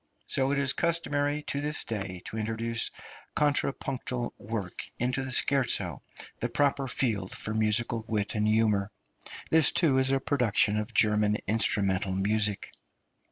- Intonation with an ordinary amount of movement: Yes, average, 4.5 semitones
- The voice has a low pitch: Yes, low, 115 Hz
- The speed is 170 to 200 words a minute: No, average, 140 wpm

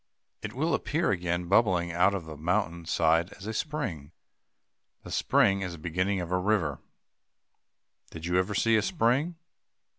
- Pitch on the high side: No, very low, 90 Hz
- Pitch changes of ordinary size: Yes, average, 4.2 semitones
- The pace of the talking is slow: No, average, 160 wpm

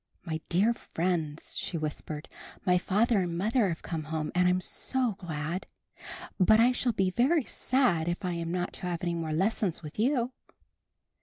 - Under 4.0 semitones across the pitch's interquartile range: No, average, 5.1 semitones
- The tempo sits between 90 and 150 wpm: No, average, 175 wpm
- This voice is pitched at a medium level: Yes, medium, 180 Hz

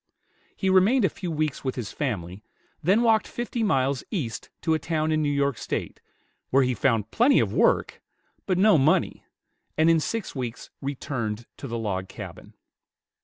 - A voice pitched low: No, medium, 145 Hz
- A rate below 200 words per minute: Yes, average, 170 wpm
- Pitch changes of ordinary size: No, wide, 7.1 semitones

